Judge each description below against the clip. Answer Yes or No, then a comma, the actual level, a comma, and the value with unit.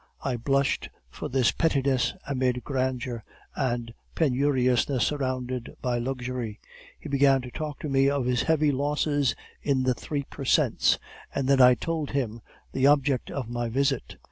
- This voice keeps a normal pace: Yes, average, 155 wpm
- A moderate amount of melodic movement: No, narrow, 2.0 semitones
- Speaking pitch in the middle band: No, low, 130 Hz